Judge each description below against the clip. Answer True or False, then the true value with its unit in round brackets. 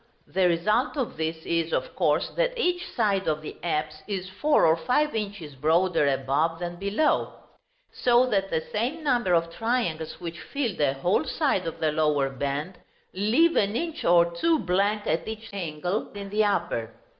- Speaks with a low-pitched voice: False (185 Hz)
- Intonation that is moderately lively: False (5.9 semitones)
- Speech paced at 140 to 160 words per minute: False (175 wpm)